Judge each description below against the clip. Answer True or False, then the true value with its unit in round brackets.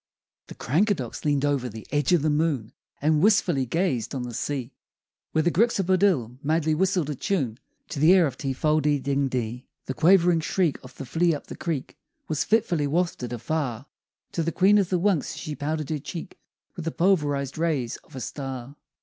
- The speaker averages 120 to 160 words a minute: False (190 wpm)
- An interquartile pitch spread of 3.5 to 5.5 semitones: True (4.3 semitones)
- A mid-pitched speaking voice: True (150 Hz)